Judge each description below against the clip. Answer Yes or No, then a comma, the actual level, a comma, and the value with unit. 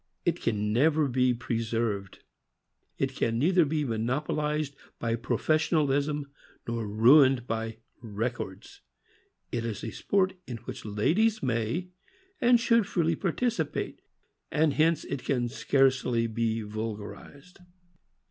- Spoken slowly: Yes, slow, 120 wpm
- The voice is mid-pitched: No, low, 125 Hz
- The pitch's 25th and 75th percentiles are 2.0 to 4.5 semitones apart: No, wide, 5.5 semitones